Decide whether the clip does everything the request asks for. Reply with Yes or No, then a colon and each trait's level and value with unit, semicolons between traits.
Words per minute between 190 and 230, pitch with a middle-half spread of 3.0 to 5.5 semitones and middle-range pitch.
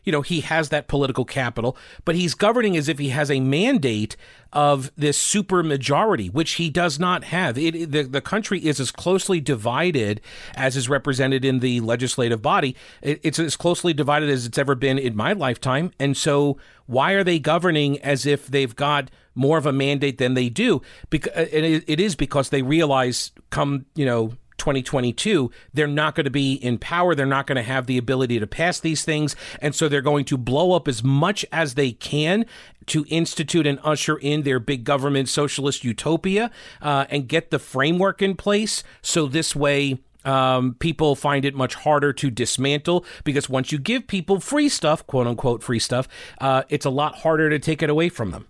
Yes: average, 200 wpm; average, 3.4 semitones; medium, 145 Hz